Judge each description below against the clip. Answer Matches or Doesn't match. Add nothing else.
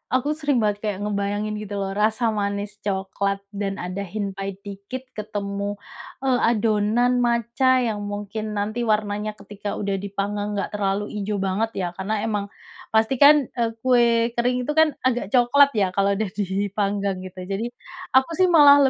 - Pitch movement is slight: Doesn't match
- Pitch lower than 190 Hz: Doesn't match